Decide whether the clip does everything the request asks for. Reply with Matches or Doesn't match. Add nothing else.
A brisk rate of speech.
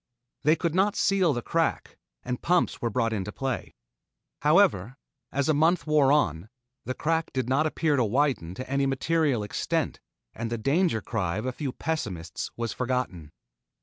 Doesn't match